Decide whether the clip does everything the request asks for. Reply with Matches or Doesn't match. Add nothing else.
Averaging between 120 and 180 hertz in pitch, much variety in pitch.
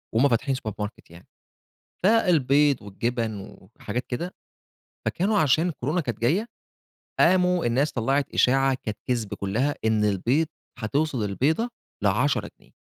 Matches